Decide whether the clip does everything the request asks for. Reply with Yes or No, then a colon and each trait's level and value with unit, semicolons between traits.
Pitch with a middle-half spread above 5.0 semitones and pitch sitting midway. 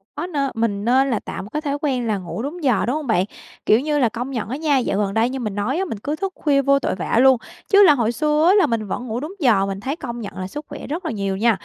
No: wide, 5.5 semitones; very high, 250 Hz